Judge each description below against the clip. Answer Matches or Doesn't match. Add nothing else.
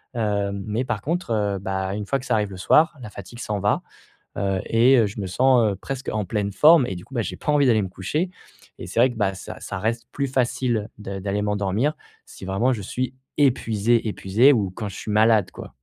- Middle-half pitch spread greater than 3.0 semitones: Matches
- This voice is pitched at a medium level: Doesn't match